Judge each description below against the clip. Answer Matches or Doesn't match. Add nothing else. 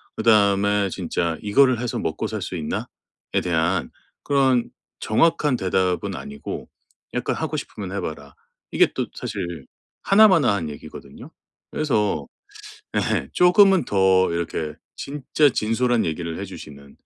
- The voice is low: Matches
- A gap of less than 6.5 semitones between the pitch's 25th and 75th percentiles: Doesn't match